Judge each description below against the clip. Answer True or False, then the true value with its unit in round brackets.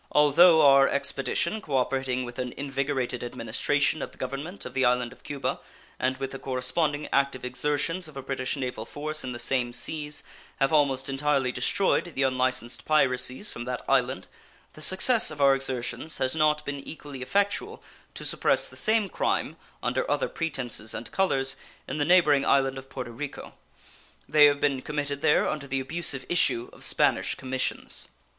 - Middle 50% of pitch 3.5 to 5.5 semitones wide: False (2.7 semitones)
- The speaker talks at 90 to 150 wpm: False (170 wpm)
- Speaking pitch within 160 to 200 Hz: False (135 Hz)